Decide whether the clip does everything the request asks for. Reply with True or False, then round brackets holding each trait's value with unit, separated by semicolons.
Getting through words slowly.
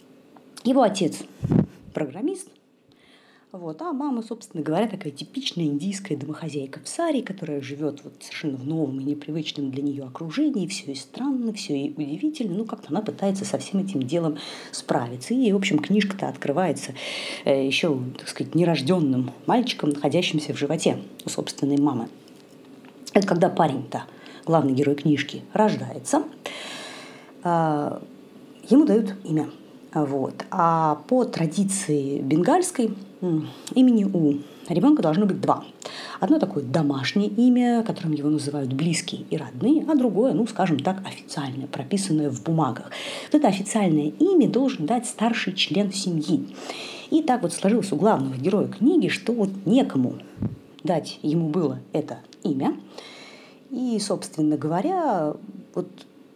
False (135 wpm)